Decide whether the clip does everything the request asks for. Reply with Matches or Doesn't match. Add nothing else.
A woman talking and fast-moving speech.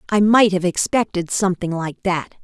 Doesn't match